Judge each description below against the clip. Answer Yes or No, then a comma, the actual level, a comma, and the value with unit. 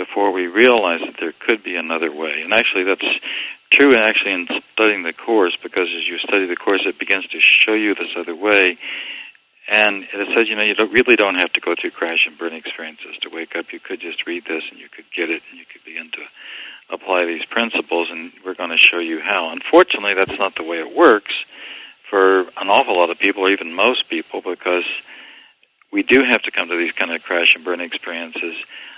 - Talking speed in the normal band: No, fast, 220 wpm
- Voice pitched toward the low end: Yes, low, 100 Hz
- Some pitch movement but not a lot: No, wide, 5.9 semitones